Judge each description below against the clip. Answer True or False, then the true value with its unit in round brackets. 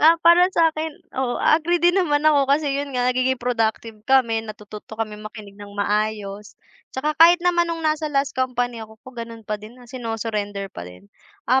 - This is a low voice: False (245 Hz)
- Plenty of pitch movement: True (5.8 semitones)